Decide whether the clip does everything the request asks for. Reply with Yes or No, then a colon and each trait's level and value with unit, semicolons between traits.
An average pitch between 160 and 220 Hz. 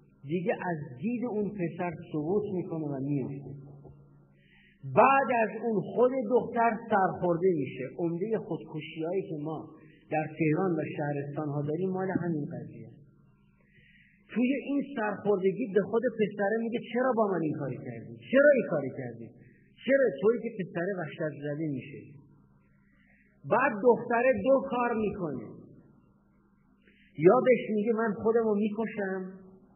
Yes: medium, 185 Hz